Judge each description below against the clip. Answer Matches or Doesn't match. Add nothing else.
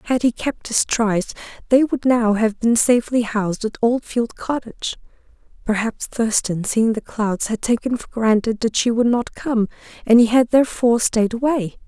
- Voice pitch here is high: Matches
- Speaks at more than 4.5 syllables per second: Matches